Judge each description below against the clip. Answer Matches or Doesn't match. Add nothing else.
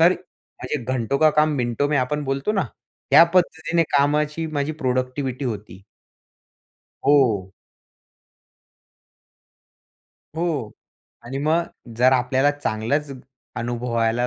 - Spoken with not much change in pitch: Doesn't match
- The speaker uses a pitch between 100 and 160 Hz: Matches